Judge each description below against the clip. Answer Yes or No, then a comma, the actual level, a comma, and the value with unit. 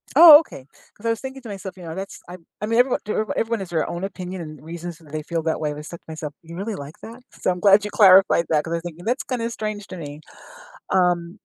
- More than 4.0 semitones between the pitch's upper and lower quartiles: Yes, average, 4.6 semitones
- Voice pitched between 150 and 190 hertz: Yes, medium, 185 Hz